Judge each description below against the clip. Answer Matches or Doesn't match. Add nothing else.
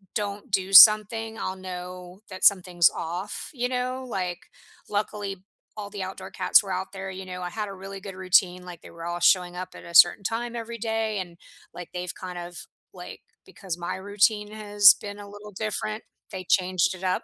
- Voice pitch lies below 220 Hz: Matches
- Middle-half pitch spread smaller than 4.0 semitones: Matches